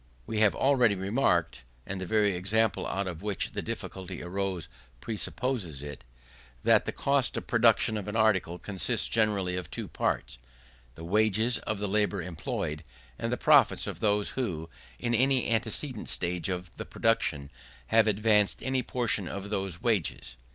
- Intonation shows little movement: No, average, 3.7 semitones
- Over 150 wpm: Yes, average, 160 wpm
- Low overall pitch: Yes, low, 105 Hz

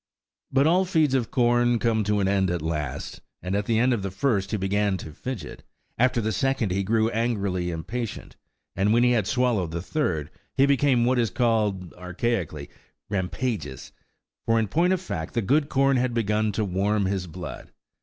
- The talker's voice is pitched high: No, low, 110 Hz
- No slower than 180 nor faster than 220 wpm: Yes, average, 190 wpm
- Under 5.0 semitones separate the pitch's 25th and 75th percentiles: Yes, average, 4.6 semitones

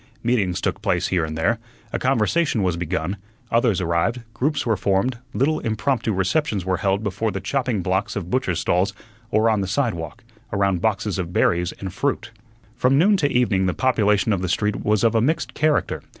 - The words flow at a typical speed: Yes, average, 190 wpm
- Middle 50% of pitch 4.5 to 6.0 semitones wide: Yes, average, 4.8 semitones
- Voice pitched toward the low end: Yes, low, 105 Hz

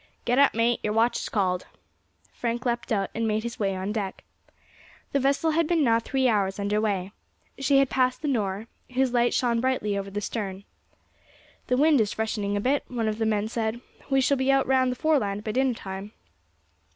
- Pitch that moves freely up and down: No, average, 4.1 semitones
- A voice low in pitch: No, high, 230 Hz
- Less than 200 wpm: No, fast, 205 wpm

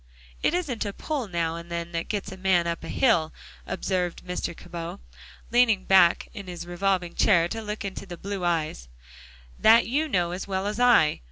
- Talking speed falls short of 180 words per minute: No, average, 185 wpm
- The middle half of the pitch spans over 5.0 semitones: No, average, 3.7 semitones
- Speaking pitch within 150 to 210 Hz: Yes, medium, 185 Hz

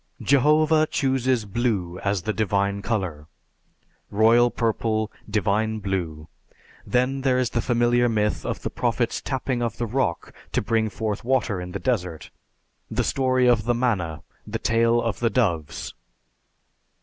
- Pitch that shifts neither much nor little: Yes, average, 3.7 semitones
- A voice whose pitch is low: Yes, low, 115 Hz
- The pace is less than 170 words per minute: Yes, average, 145 wpm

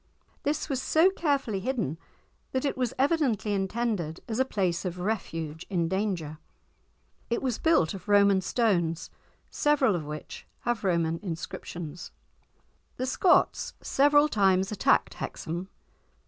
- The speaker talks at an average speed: No, slow, 130 wpm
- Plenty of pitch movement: Yes, wide, 7.1 semitones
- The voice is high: Yes, high, 200 Hz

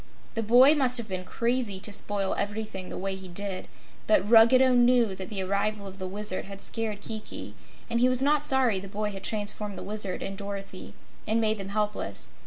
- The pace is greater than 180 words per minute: Yes, average, 200 wpm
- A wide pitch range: No, average, 3.1 semitones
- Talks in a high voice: Yes, high, 210 Hz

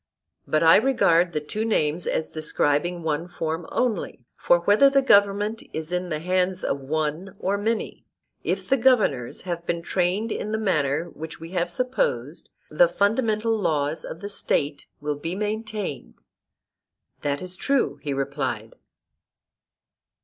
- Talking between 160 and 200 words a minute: No, average, 150 wpm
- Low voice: No, medium, 175 Hz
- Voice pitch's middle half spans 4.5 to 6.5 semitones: Yes, wide, 5.5 semitones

